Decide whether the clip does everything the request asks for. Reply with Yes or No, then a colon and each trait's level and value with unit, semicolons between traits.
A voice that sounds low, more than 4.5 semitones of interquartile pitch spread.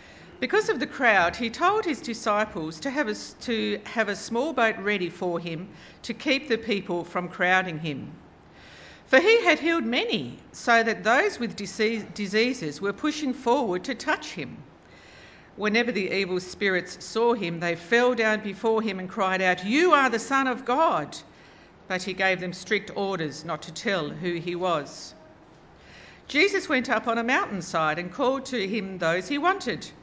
No: high, 215 Hz; wide, 5.4 semitones